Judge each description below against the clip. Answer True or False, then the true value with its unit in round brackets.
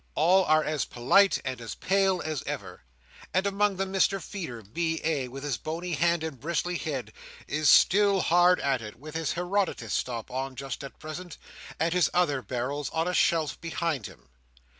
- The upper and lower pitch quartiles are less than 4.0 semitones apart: False (4.7 semitones)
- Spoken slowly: False (180 wpm)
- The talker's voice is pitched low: False (160 Hz)